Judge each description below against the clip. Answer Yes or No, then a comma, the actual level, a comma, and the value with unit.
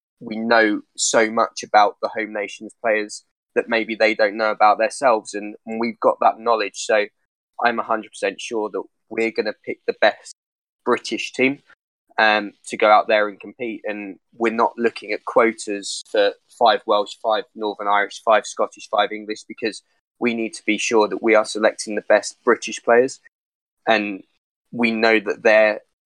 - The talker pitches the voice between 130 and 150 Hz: No, low, 110 Hz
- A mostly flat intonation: Yes, narrow, 1.4 semitones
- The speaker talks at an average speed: Yes, average, 175 wpm